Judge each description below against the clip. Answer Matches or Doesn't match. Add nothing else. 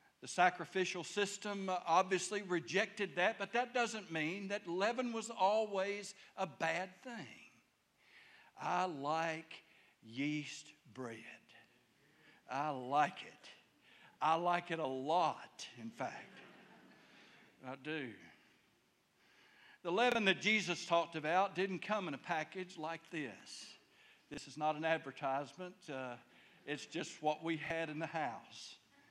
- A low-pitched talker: Doesn't match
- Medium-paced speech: Doesn't match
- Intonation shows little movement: Doesn't match